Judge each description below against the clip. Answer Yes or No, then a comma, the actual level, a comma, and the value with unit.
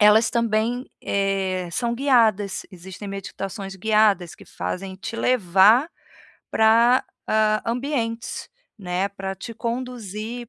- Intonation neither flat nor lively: Yes, average, 3.3 semitones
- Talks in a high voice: Yes, high, 215 Hz